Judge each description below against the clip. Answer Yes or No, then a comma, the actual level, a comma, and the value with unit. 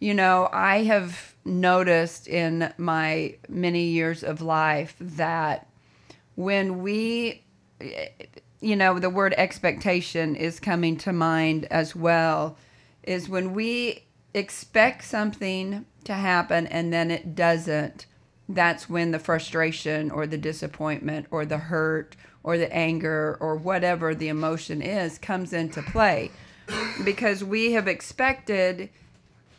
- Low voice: No, medium, 170 Hz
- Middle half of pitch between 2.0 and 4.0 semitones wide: Yes, average, 3.1 semitones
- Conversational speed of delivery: No, slow, 125 wpm